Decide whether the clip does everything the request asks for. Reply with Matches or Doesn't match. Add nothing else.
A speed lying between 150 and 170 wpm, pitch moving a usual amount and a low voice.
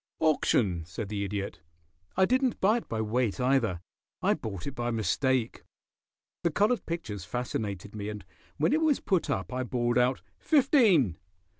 Doesn't match